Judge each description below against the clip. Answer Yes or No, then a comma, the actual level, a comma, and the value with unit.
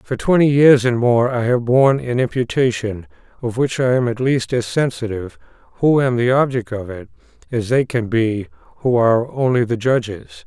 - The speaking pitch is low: Yes, low, 120 Hz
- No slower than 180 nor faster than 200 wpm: Yes, average, 190 wpm